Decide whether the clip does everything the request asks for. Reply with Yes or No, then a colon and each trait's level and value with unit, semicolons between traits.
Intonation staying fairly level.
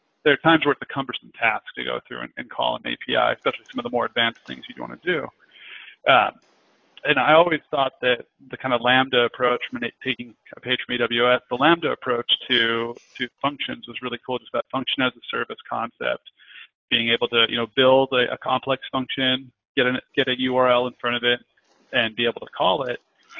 Yes: narrow, 1.4 semitones